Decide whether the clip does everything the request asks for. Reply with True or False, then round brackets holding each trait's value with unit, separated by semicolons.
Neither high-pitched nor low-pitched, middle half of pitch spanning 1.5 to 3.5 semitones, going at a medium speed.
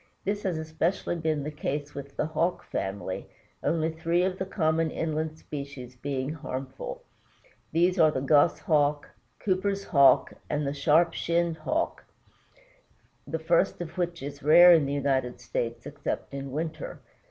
True (155 Hz; 3.1 semitones; 150 wpm)